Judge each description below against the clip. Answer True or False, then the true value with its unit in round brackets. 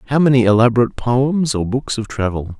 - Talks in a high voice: False (120 Hz)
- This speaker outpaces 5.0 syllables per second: True (5.9 syllables/s)